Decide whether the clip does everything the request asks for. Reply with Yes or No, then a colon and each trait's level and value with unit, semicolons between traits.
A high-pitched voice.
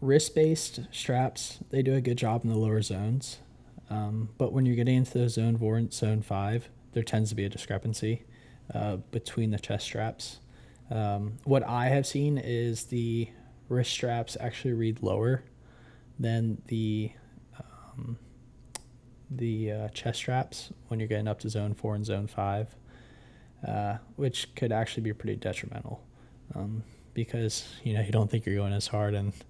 No: low, 115 Hz